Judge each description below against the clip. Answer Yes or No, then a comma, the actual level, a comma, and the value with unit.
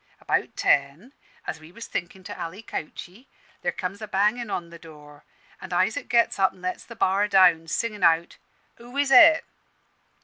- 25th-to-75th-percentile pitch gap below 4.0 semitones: No, wide, 5.4 semitones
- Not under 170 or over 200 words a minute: Yes, average, 175 wpm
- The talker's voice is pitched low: No, high, 190 Hz